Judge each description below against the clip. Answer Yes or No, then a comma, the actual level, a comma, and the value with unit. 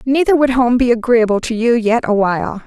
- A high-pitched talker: Yes, high, 235 Hz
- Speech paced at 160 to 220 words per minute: Yes, average, 200 wpm